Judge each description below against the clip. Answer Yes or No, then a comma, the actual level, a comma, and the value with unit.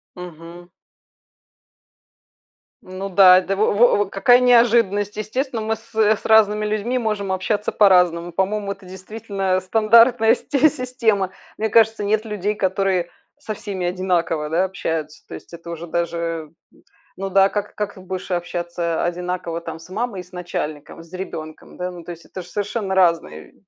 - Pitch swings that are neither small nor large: Yes, average, 3.5 semitones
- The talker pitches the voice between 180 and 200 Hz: Yes, high, 190 Hz